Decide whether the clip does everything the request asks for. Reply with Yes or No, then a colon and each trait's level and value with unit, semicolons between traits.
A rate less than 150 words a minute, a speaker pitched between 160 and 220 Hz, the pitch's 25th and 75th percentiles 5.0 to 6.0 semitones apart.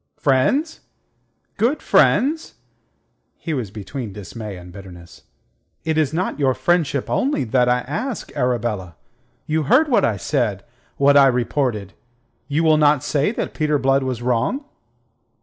No: average, 140 wpm; low, 135 Hz; wide, 5.6 semitones